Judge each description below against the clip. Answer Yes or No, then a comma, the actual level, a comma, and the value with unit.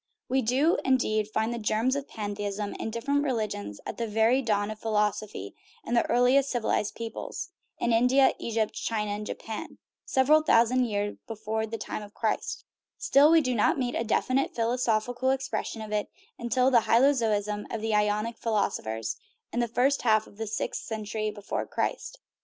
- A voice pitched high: Yes, high, 225 Hz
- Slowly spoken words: No, average, 175 wpm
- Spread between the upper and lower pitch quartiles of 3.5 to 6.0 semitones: No, average, 3.0 semitones